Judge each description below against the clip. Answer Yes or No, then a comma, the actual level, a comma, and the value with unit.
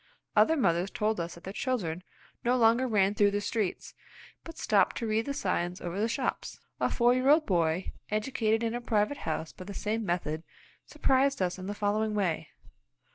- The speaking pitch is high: Yes, high, 210 Hz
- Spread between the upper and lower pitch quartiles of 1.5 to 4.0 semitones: No, average, 4.5 semitones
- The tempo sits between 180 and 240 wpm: Yes, average, 190 wpm